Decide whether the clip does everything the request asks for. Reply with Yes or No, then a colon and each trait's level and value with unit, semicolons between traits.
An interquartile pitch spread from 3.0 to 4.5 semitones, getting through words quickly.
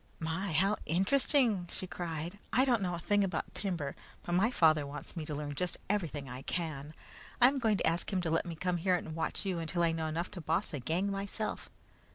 Yes: average, 3.7 semitones; fast, 225 wpm